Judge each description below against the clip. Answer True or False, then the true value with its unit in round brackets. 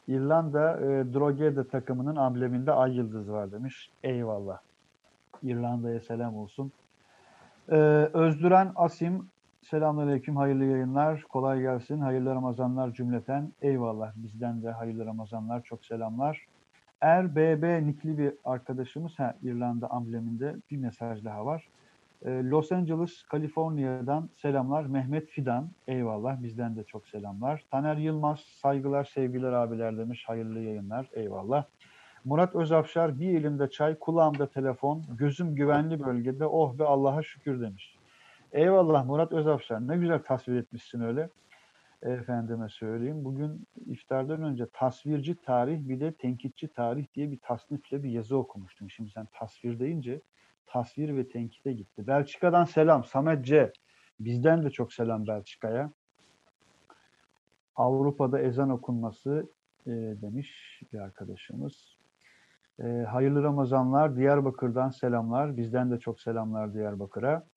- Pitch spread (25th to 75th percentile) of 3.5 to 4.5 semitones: True (4.1 semitones)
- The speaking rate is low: False (120 wpm)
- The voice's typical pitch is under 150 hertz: True (135 Hz)